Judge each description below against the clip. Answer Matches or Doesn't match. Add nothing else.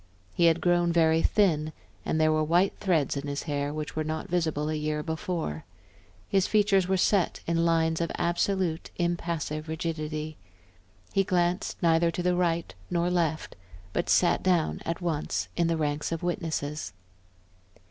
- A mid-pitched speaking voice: Matches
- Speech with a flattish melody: Matches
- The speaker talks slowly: Doesn't match